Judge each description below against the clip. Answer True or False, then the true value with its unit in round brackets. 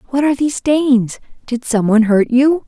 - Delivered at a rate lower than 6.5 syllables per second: True (5.5 syllables/s)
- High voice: True (255 Hz)